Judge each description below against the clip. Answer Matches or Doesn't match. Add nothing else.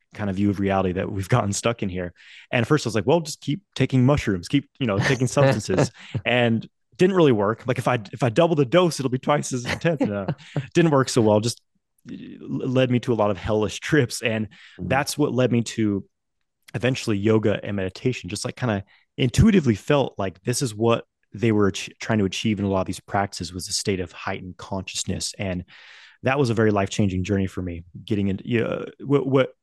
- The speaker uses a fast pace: Matches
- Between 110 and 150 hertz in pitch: Matches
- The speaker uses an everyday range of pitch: Matches